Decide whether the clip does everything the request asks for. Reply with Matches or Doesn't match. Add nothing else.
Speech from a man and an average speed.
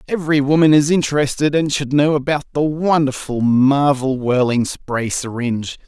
Matches